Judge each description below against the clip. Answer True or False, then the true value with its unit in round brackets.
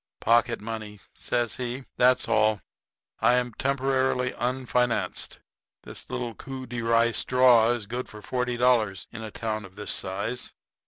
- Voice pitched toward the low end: True (120 Hz)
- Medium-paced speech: True (150 wpm)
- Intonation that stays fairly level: True (2.3 semitones)